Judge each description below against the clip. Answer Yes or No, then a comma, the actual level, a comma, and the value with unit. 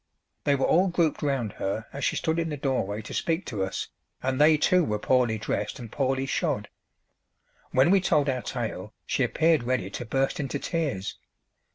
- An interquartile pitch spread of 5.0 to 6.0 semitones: Yes, wide, 5.4 semitones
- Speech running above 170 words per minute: Yes, average, 190 wpm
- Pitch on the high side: No, low, 135 Hz